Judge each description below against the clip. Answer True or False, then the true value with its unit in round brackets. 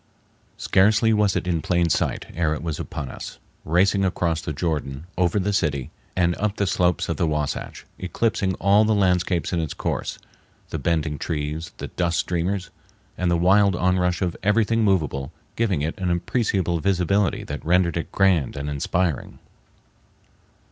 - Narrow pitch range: False (3.3 semitones)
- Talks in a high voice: False (90 Hz)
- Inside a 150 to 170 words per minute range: True (160 wpm)